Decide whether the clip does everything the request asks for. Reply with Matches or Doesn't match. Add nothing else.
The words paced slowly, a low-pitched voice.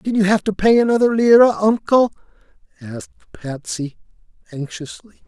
Doesn't match